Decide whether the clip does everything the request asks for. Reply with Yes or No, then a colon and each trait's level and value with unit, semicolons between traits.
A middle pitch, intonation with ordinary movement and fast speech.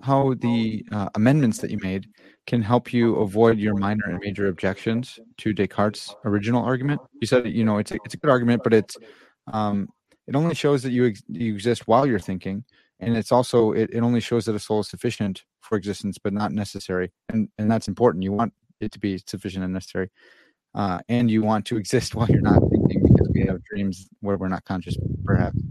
No: low, 110 Hz; average, 3.0 semitones; fast, 215 wpm